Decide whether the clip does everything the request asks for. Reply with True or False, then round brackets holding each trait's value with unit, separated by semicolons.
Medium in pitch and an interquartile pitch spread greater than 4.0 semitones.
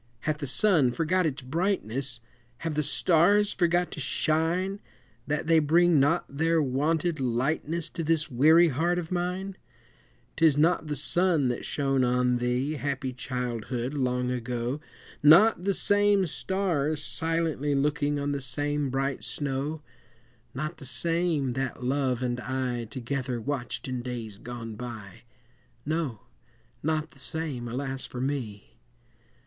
True (145 Hz; 4.5 semitones)